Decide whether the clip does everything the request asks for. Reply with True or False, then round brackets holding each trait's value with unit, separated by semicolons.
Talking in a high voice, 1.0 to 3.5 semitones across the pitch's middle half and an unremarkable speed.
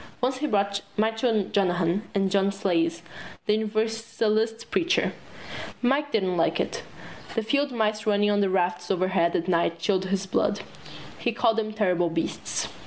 True (205 Hz; 3.2 semitones; 155 wpm)